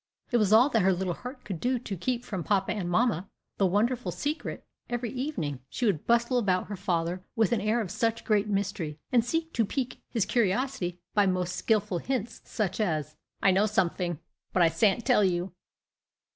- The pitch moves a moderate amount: Yes, average, 4.6 semitones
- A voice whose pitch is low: No, high, 210 Hz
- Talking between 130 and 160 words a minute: No, average, 195 wpm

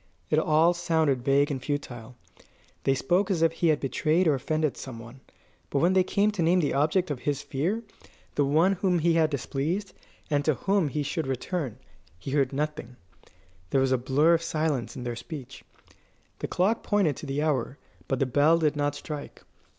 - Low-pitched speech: No, medium, 150 Hz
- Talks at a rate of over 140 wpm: Yes, average, 195 wpm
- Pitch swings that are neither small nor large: Yes, average, 3.6 semitones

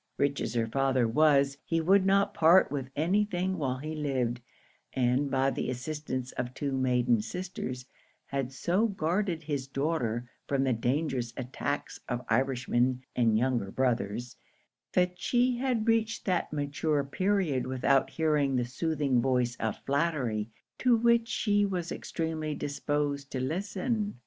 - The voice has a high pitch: No, medium, 140 Hz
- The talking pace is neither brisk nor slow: Yes, average, 145 wpm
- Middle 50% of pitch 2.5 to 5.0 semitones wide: No, wide, 5.4 semitones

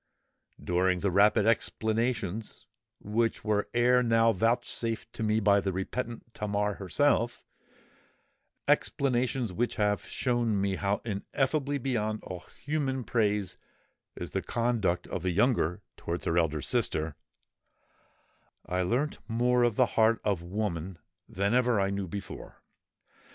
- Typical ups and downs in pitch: Yes, average, 3.7 semitones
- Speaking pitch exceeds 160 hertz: No, low, 110 Hz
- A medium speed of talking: No, slow, 125 wpm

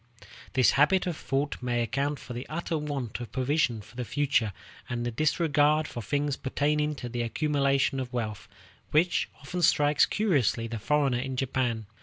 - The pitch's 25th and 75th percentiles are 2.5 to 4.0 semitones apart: Yes, average, 3.6 semitones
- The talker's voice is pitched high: No, low, 135 Hz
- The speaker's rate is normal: Yes, average, 170 wpm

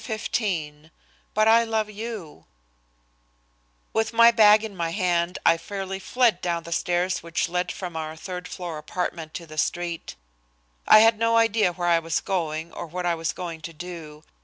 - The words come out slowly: No, average, 175 wpm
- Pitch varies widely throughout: No, average, 4.3 semitones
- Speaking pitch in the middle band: Yes, medium, 180 Hz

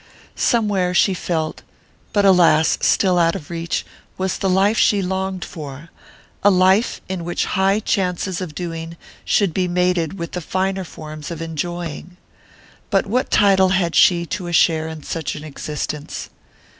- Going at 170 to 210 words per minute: No, average, 155 wpm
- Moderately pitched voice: Yes, medium, 180 Hz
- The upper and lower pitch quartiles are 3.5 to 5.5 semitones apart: No, narrow, 2.6 semitones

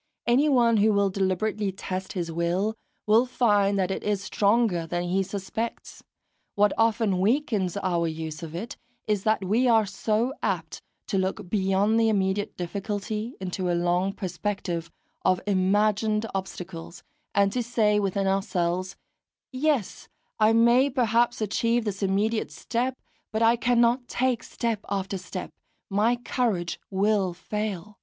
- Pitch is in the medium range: No, high, 205 Hz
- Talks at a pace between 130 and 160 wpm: Yes, average, 140 wpm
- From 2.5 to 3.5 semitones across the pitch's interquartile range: Yes, average, 3.2 semitones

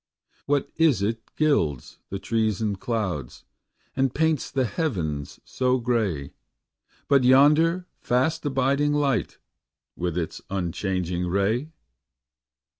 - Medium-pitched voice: No, low, 120 Hz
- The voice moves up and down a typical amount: No, wide, 7.2 semitones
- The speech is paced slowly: Yes, slow, 110 wpm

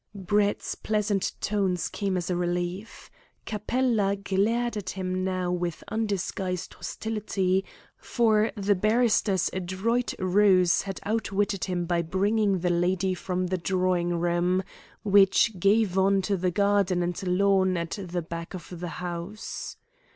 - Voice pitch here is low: No, high, 190 Hz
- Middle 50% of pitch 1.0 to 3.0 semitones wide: Yes, narrow, 2.4 semitones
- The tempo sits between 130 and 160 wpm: Yes, slow, 135 wpm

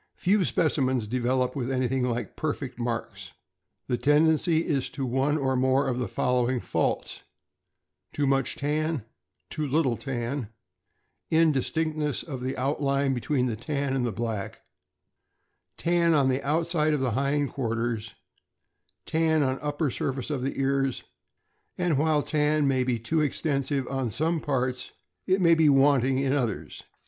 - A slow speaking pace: No, average, 145 wpm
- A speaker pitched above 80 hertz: Yes, low, 135 Hz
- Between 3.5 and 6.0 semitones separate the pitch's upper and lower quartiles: No, average, 3.0 semitones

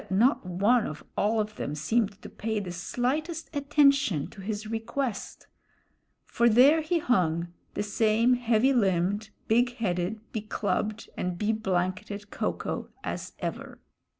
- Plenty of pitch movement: No, average, 4.2 semitones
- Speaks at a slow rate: No, average, 150 wpm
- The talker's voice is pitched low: No, high, 215 Hz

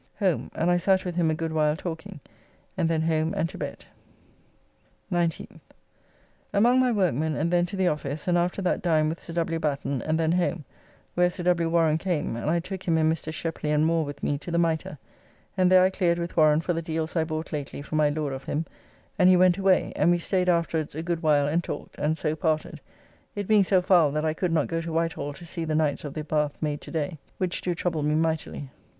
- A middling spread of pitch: No, narrow, 2.3 semitones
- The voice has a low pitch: No, medium, 165 Hz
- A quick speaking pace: Yes, fast, 235 wpm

